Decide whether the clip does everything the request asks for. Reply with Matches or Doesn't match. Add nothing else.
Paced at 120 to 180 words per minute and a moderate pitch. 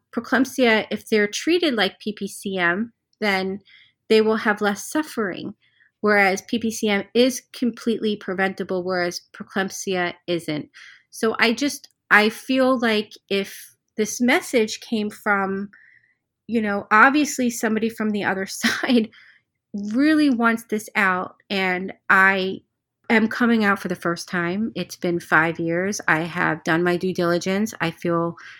Doesn't match